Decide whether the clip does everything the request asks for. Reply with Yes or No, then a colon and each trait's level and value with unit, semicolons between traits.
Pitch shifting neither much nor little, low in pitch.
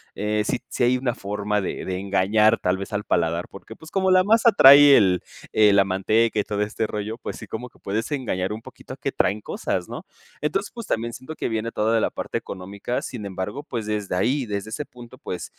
Yes: average, 3.9 semitones; low, 110 Hz